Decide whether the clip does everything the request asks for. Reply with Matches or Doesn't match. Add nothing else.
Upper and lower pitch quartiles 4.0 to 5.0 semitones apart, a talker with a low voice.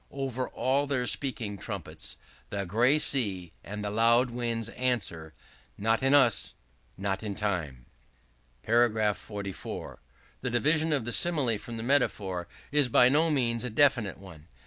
Matches